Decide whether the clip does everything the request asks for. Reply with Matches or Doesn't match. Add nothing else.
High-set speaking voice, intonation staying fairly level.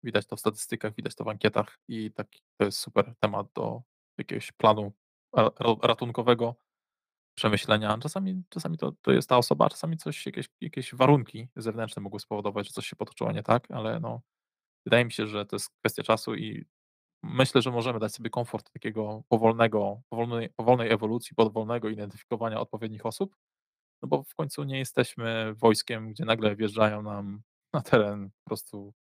Doesn't match